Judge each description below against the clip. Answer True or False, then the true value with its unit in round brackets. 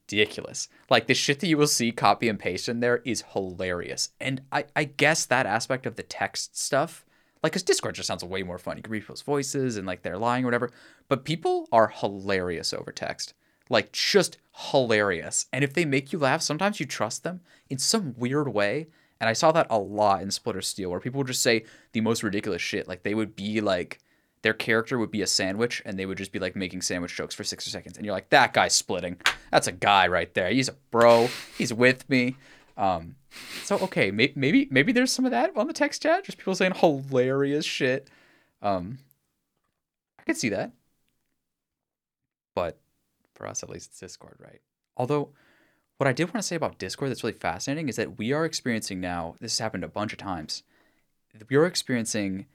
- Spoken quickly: True (210 wpm)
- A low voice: True (125 Hz)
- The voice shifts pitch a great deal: True (5.8 semitones)